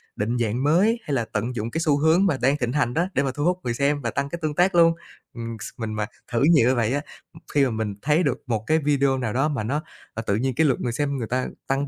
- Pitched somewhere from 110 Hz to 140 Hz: Yes, low, 135 Hz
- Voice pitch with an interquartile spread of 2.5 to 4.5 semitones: Yes, average, 4.0 semitones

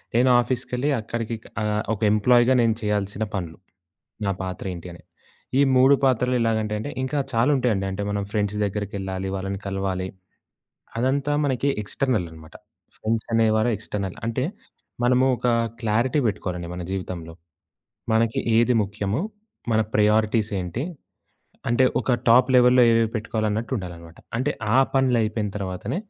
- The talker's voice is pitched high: No, low, 110 Hz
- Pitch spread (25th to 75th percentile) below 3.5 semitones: No, average, 4.0 semitones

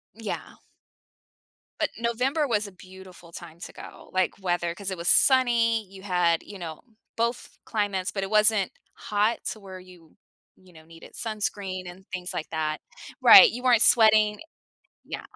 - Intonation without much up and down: No, average, 3.6 semitones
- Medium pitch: No, high, 195 Hz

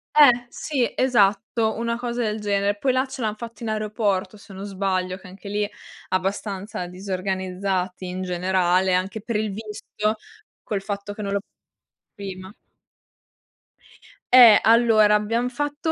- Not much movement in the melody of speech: No, average, 3.3 semitones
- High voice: Yes, high, 205 Hz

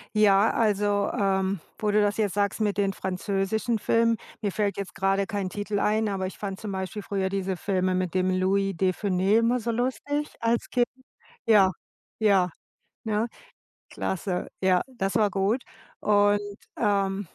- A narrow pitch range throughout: Yes, narrow, 1.9 semitones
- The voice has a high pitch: Yes, high, 200 Hz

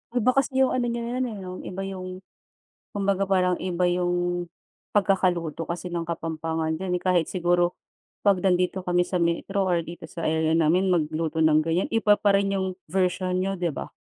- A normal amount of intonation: No, narrow, 2.3 semitones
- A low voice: No, medium, 180 Hz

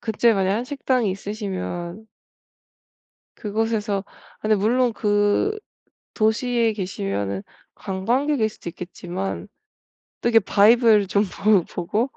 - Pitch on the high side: Yes, high, 210 Hz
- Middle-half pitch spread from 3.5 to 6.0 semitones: No, average, 3.1 semitones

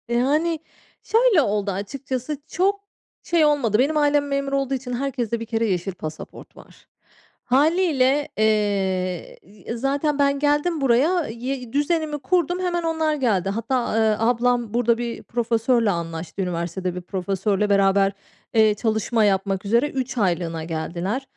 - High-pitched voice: Yes, high, 240 Hz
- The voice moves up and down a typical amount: No, wide, 6.1 semitones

